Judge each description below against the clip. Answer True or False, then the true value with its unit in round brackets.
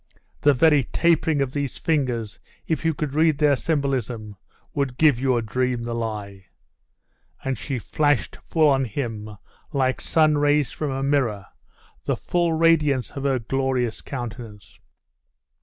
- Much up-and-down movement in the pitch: False (3.9 semitones)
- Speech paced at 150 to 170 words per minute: False (140 wpm)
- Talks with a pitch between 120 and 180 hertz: True (135 Hz)